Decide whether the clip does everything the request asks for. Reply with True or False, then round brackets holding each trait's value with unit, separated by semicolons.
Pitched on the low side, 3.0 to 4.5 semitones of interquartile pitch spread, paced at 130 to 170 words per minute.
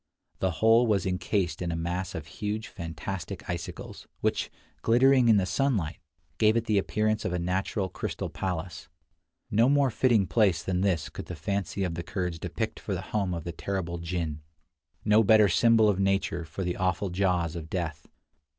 False (95 Hz; 3.8 semitones; 180 wpm)